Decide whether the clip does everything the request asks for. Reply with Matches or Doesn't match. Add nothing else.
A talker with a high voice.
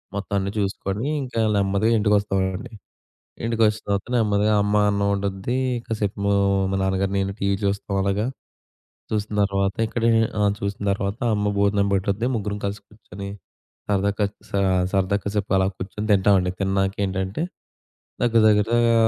Doesn't match